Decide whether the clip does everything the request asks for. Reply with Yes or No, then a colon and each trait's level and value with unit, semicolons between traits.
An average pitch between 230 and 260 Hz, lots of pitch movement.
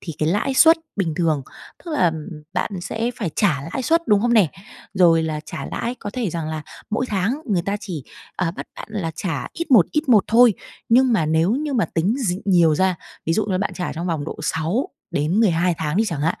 No: high, 190 Hz; wide, 5.8 semitones